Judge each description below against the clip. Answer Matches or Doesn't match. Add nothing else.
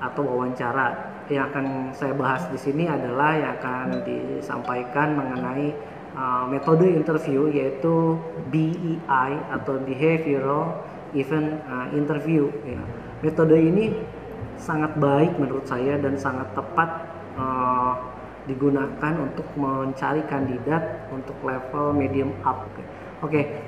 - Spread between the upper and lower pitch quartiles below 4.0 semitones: Matches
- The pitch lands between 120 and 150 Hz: Matches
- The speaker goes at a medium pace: Matches